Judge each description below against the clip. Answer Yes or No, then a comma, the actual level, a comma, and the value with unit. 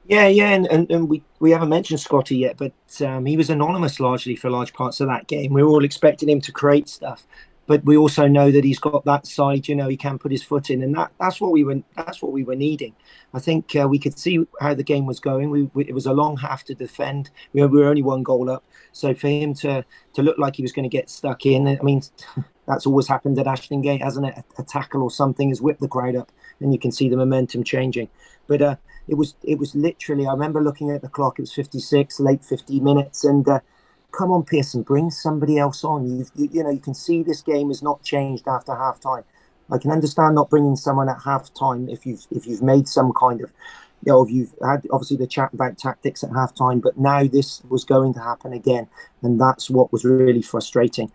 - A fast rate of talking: Yes, fast, 250 wpm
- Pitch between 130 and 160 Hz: Yes, medium, 140 Hz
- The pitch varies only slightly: Yes, narrow, 2.1 semitones